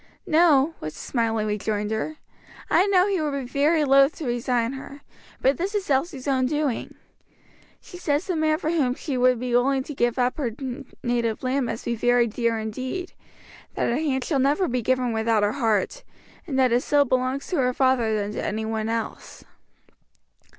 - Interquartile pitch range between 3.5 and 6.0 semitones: Yes, average, 3.8 semitones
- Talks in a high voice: Yes, very high, 255 Hz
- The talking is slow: No, average, 190 wpm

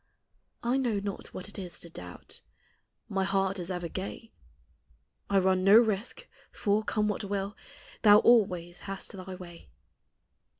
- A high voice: Yes, high, 195 Hz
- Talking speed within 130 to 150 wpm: Yes, average, 145 wpm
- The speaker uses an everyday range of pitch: No, narrow, 2.2 semitones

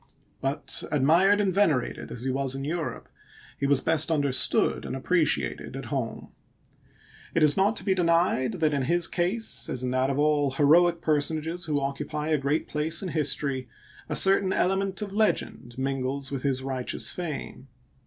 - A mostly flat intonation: No, average, 4.2 semitones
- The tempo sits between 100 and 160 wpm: No, average, 170 wpm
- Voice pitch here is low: No, medium, 150 Hz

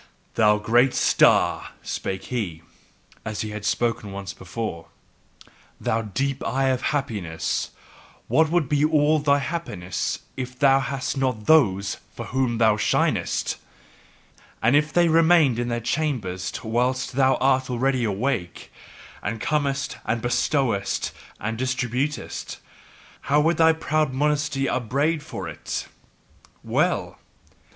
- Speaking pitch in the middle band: No, low, 130 Hz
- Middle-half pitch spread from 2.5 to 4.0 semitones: No, average, 4.7 semitones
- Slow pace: Yes, slow, 125 wpm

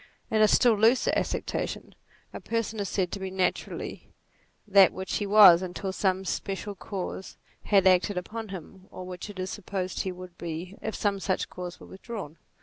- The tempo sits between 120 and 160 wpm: No, average, 180 wpm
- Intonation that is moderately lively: No, narrow, 2.0 semitones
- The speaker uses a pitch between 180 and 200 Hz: Yes, high, 190 Hz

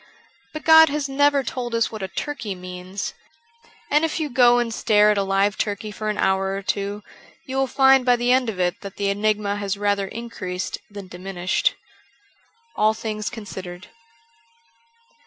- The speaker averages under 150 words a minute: No, average, 175 wpm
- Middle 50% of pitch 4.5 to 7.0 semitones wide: No, average, 3.9 semitones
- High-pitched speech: Yes, high, 210 Hz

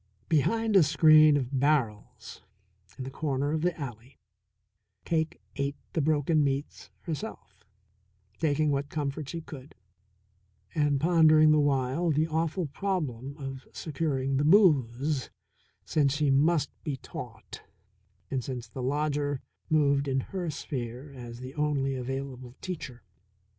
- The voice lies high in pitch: No, medium, 145 Hz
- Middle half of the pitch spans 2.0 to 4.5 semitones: Yes, average, 2.7 semitones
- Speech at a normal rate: No, slow, 130 wpm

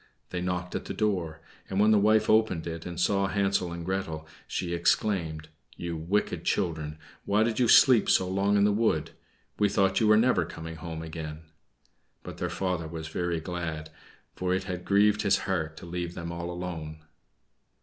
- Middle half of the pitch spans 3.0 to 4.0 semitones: Yes, average, 3.6 semitones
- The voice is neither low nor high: No, very low, 90 Hz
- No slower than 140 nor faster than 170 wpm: No, average, 185 wpm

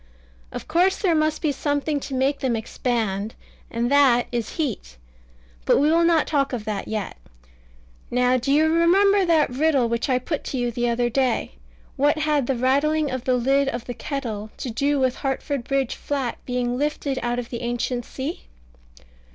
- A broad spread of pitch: No, average, 3.5 semitones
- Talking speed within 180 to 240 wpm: Yes, average, 185 wpm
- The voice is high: Yes, very high, 265 Hz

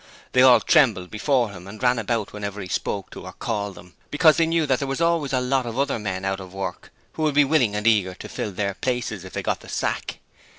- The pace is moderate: No, fast, 255 wpm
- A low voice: Yes, low, 115 Hz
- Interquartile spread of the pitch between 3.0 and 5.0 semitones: No, wide, 5.6 semitones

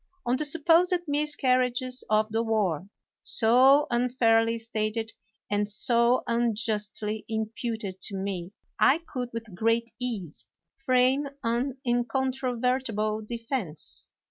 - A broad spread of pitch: No, average, 2.8 semitones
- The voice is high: Yes, high, 235 Hz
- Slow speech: Yes, slow, 110 wpm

